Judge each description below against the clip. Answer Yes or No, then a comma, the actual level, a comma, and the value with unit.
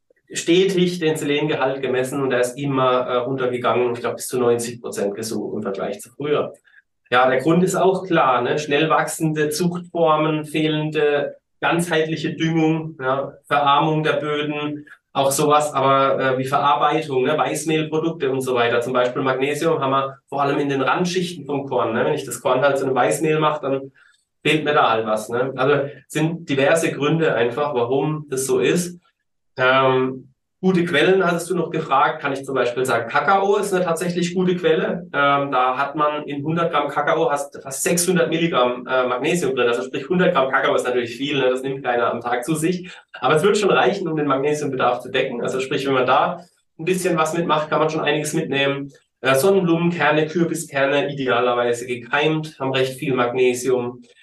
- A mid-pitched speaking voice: Yes, medium, 145 Hz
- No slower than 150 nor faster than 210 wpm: Yes, average, 185 wpm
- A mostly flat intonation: No, average, 3.5 semitones